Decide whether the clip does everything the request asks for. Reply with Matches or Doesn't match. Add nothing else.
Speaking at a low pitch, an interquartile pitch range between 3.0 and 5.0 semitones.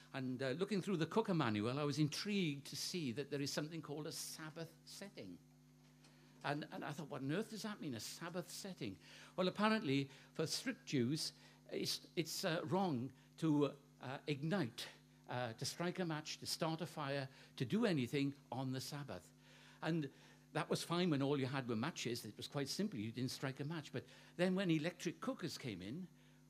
Doesn't match